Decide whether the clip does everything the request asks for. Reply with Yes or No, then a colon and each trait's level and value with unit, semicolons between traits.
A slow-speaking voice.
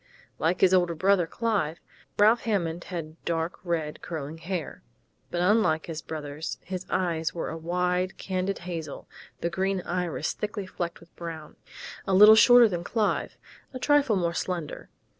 No: average, 155 wpm